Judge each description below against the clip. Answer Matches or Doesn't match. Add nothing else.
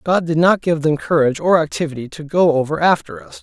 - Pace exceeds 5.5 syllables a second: Matches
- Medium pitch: Matches